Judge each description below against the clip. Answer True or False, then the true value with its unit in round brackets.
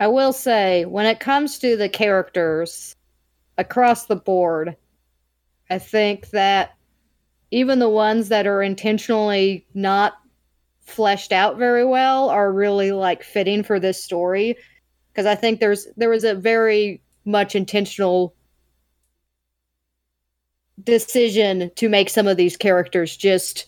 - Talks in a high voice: True (200 Hz)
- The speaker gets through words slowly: True (130 wpm)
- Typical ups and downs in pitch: True (3.6 semitones)